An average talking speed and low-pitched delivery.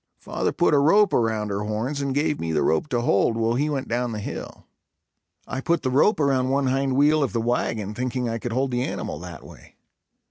No: fast, 225 wpm; low, 130 Hz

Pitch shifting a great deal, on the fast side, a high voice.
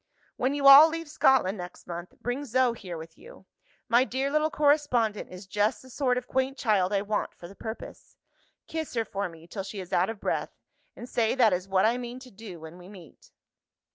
Yes: wide, 5.7 semitones; fast, 215 wpm; high, 225 Hz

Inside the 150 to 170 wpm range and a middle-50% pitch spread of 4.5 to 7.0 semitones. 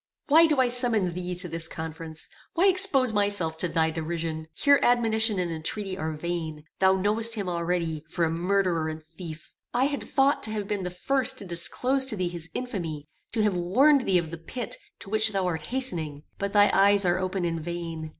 No: fast, 205 wpm; average, 5.2 semitones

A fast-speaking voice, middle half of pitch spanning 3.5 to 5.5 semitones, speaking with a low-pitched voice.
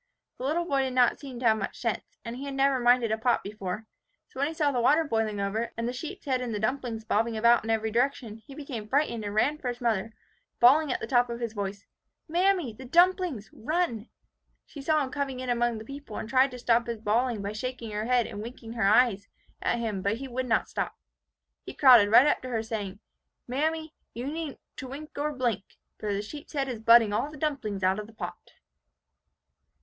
No: fast, 225 wpm; average, 4.0 semitones; high, 240 Hz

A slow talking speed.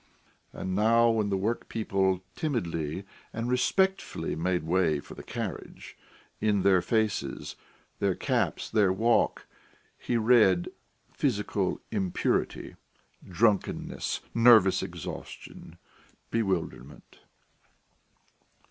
Yes: slow, 90 wpm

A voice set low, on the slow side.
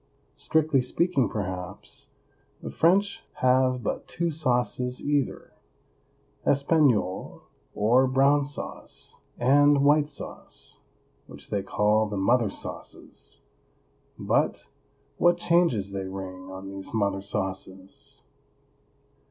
Yes: low, 125 Hz; slow, 100 wpm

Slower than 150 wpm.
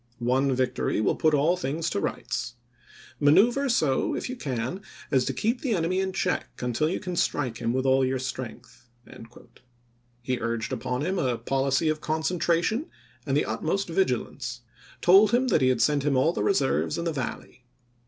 No: average, 175 wpm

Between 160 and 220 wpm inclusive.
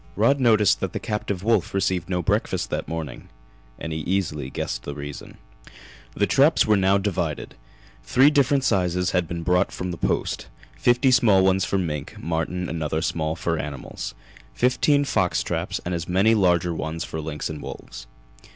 Yes: average, 175 wpm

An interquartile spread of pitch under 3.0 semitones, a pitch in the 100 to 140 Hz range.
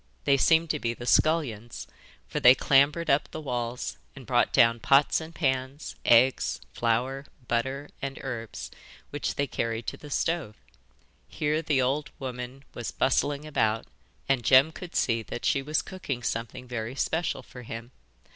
No: average, 3.6 semitones; low, 135 Hz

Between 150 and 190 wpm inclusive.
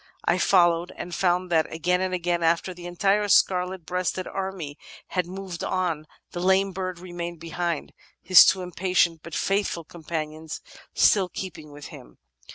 Yes: average, 160 wpm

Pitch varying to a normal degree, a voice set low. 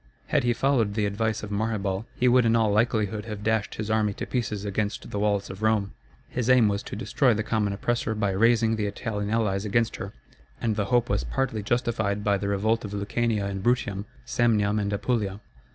No: narrow, 2.1 semitones; low, 105 Hz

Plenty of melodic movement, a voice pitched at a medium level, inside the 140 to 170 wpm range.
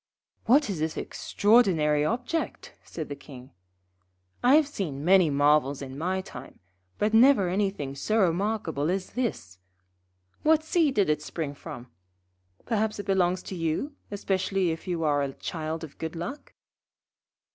Yes: wide, 5.9 semitones; medium, 180 Hz; average, 145 wpm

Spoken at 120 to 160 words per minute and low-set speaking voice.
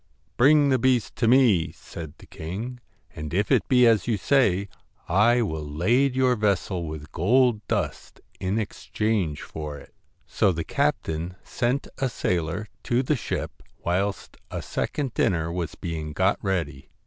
Yes: average, 155 wpm; low, 100 Hz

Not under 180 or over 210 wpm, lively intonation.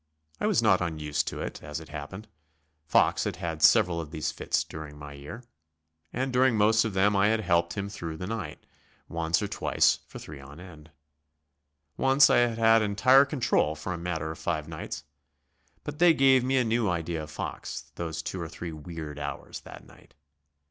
Yes: average, 195 wpm; wide, 6.2 semitones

